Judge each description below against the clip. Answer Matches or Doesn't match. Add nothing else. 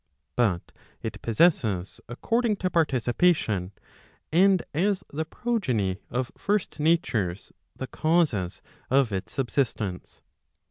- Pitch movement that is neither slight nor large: Doesn't match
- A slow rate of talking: Matches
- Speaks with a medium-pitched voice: Doesn't match